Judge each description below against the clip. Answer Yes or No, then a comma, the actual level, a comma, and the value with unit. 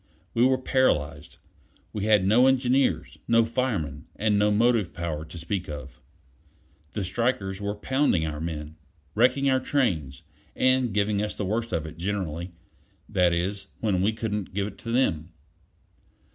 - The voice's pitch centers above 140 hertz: No, low, 100 Hz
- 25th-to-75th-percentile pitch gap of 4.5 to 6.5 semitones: Yes, wide, 5.6 semitones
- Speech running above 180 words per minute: No, average, 155 wpm